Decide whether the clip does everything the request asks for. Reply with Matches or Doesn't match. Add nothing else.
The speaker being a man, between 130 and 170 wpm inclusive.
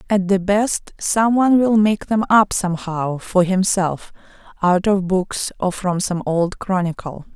Doesn't match